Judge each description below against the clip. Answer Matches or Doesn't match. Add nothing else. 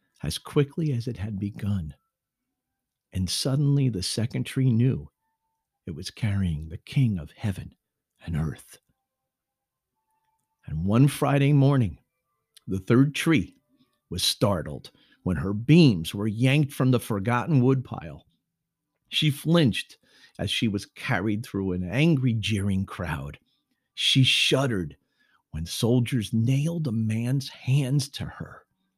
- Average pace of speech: Doesn't match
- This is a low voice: Matches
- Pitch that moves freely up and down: Matches